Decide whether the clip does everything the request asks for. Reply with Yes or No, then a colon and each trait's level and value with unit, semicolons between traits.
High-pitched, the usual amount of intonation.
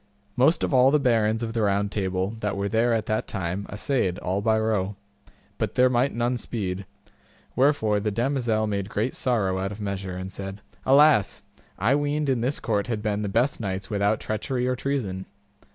No: low, 110 Hz; average, 3.9 semitones